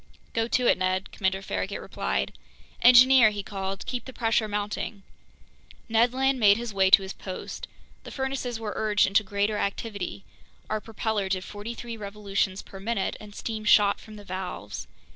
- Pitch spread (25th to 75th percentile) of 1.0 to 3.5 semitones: Yes, average, 2.9 semitones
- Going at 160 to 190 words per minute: Yes, average, 170 wpm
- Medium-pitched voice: No, high, 210 Hz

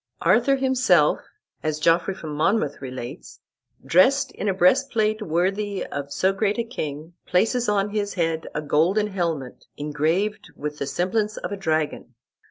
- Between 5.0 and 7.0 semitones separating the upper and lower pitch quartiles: Yes, wide, 5.6 semitones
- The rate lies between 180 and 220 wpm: No, average, 150 wpm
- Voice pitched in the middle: Yes, medium, 180 Hz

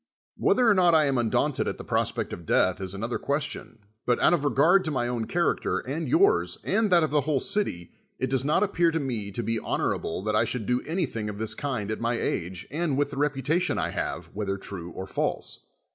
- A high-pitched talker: No, low, 135 Hz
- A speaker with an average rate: No, fast, 230 wpm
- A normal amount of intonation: No, wide, 7.0 semitones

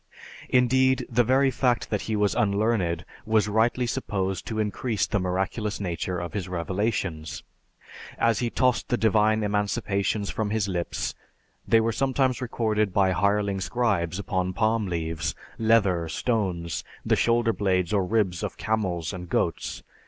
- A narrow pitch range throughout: No, average, 3.6 semitones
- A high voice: No, low, 105 Hz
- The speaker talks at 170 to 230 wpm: No, average, 145 wpm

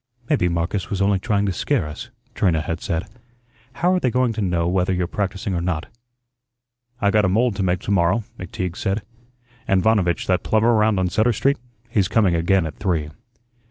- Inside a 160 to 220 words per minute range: Yes, average, 195 wpm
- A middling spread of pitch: Yes, average, 3.6 semitones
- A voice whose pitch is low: Yes, very low, 95 Hz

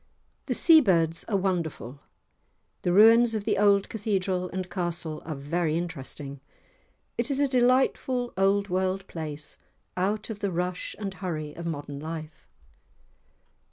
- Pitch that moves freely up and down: No, average, 4.2 semitones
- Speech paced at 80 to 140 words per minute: Yes, slow, 135 wpm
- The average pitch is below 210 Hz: Yes, medium, 185 Hz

